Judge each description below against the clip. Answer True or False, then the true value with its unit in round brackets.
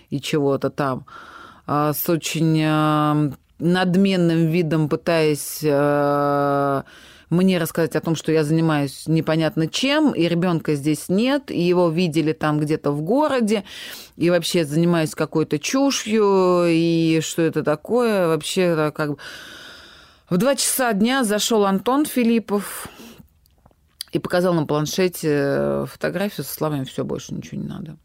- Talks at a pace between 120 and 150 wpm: True (125 wpm)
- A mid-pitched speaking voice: True (165 Hz)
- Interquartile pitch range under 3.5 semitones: False (3.8 semitones)